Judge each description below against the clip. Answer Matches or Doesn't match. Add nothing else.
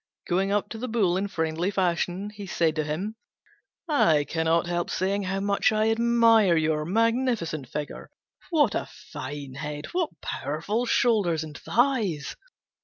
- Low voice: Doesn't match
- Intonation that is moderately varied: Doesn't match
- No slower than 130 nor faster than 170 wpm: Matches